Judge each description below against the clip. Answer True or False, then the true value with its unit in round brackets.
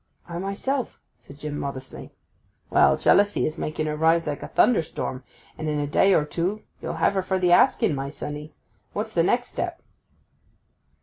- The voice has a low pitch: False (155 Hz)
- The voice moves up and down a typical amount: True (4.3 semitones)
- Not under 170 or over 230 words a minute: True (175 wpm)